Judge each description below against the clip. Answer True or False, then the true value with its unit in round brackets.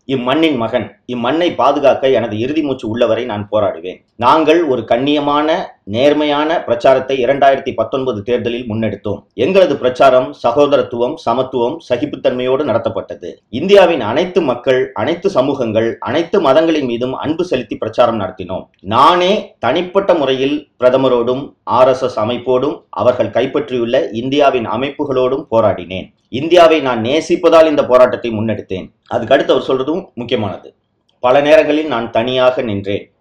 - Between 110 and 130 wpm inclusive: True (115 wpm)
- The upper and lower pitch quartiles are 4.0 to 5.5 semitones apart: False (3.6 semitones)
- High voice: False (125 Hz)